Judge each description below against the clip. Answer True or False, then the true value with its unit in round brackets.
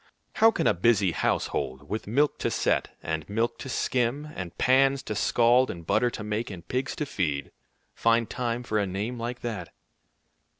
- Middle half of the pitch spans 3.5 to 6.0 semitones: True (4.4 semitones)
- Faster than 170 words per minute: True (180 wpm)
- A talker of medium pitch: False (115 Hz)